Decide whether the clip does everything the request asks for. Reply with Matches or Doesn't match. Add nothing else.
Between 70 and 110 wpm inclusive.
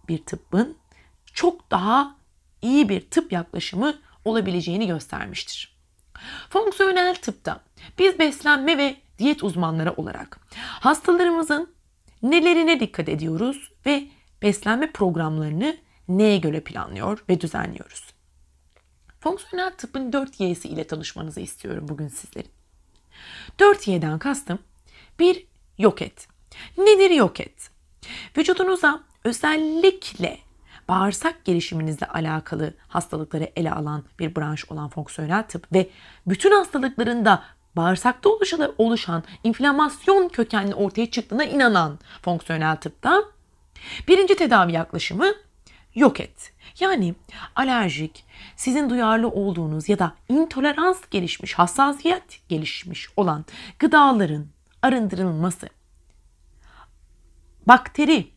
Matches